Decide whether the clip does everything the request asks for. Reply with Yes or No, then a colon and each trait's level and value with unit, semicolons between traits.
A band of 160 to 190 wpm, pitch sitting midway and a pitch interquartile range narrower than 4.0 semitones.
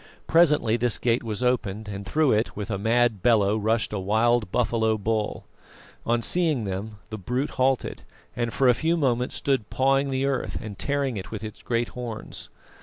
No: average, 185 wpm; low, 115 Hz; average, 3.3 semitones